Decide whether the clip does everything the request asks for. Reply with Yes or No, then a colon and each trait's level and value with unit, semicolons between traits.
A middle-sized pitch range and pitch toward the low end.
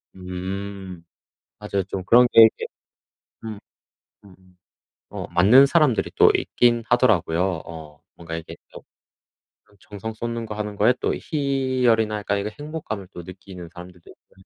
Yes: average, 4.2 semitones; low, 100 Hz